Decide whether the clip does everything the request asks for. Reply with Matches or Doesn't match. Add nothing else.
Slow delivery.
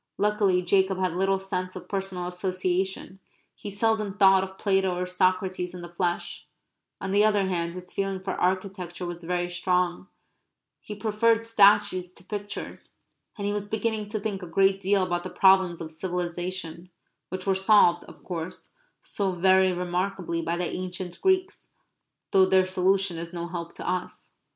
Doesn't match